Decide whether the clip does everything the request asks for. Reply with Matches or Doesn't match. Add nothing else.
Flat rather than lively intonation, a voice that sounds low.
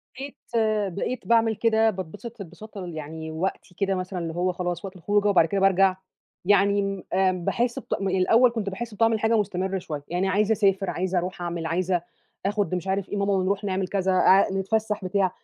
Doesn't match